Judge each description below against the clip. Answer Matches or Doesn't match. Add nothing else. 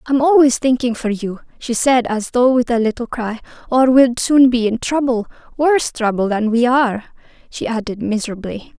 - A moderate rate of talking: Matches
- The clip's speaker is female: Matches